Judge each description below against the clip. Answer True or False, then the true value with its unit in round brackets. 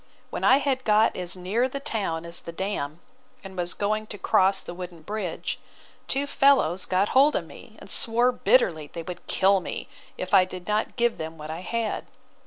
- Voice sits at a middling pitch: False (195 Hz)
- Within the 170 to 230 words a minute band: True (195 wpm)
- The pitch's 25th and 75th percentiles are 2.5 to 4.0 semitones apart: False (4.9 semitones)